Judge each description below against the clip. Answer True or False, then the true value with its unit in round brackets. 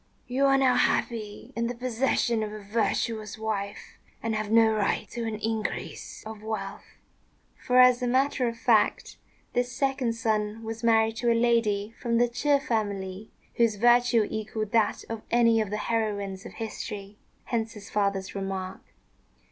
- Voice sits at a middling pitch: False (225 Hz)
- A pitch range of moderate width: False (2.2 semitones)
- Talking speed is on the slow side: False (165 wpm)